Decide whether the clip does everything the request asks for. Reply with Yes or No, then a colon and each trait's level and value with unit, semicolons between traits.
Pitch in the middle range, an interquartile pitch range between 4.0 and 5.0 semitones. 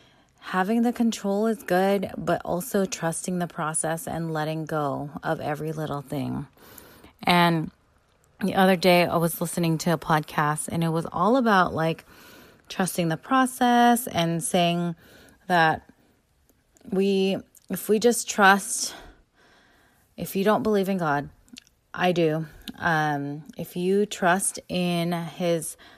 No: medium, 175 Hz; average, 3.6 semitones